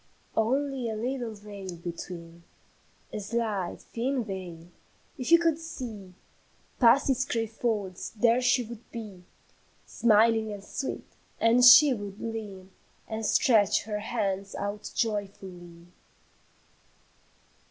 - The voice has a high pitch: Yes, high, 220 Hz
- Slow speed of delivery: Yes, slow, 115 wpm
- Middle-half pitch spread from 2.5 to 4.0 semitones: Yes, average, 3.5 semitones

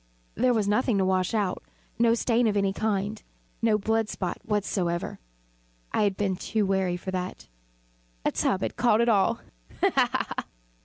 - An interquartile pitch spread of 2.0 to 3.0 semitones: Yes, average, 2.7 semitones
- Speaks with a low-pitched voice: No, high, 205 Hz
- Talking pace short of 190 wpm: Yes, average, 160 wpm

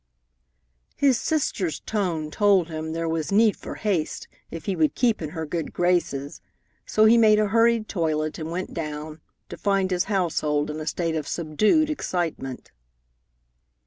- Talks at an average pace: Yes, average, 160 wpm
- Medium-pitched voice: Yes, medium, 170 Hz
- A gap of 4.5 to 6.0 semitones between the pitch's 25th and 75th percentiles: Yes, average, 5.1 semitones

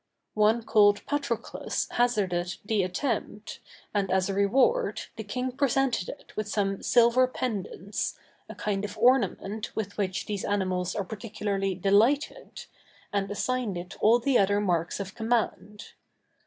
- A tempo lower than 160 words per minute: Yes, average, 140 wpm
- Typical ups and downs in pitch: Yes, average, 3.5 semitones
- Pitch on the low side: No, high, 210 Hz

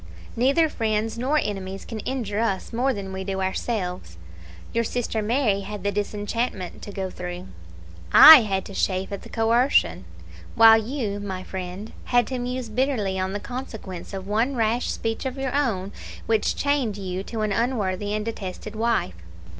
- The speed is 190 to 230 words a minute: No, average, 170 wpm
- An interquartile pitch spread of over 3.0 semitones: Yes, average, 4.0 semitones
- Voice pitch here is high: Yes, high, 215 Hz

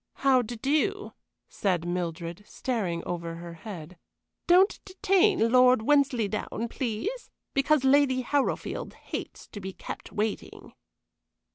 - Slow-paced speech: Yes, slow, 115 wpm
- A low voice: No, high, 235 Hz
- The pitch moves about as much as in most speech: No, wide, 7.7 semitones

